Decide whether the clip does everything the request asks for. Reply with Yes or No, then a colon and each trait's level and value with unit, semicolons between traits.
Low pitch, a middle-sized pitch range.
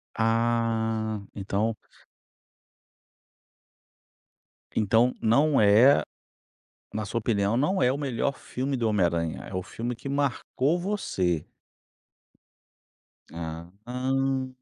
Yes: low, 115 Hz; average, 4.3 semitones